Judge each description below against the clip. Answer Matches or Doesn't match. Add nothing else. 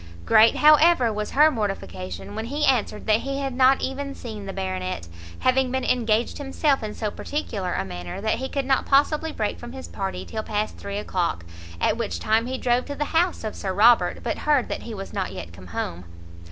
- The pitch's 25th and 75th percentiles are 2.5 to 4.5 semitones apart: Doesn't match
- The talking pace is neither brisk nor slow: Doesn't match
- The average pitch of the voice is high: Matches